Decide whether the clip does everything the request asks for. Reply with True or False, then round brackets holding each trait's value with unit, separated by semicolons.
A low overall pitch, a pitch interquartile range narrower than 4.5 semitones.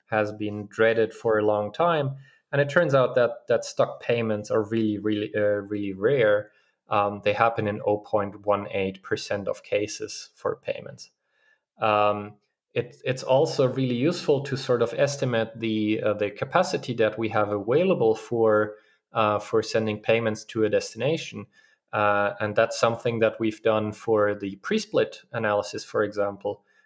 True (110 Hz; 3.2 semitones)